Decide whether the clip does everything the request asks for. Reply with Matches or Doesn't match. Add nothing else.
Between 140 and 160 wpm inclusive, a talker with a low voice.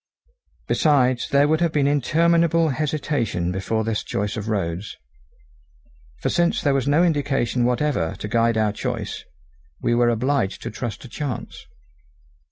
Matches